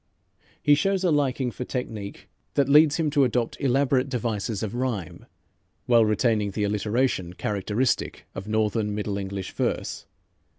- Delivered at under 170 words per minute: Yes, average, 140 wpm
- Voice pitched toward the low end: Yes, low, 115 Hz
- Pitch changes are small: No, average, 4.4 semitones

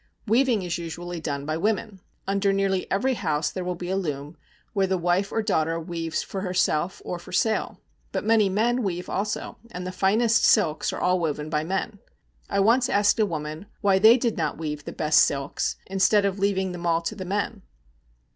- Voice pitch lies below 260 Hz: Yes, high, 190 Hz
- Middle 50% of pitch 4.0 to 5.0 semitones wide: No, average, 3.6 semitones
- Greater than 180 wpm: Yes, average, 200 wpm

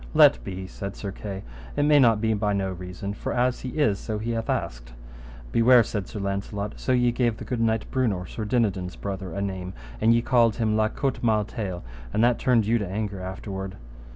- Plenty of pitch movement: No, average, 3.3 semitones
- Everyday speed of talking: No, fast, 215 wpm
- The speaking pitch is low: Yes, low, 105 Hz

